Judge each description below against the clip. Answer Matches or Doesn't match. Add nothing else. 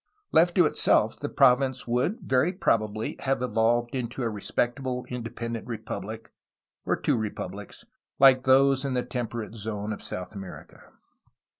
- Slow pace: Doesn't match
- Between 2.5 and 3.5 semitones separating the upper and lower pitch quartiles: Matches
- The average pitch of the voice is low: Matches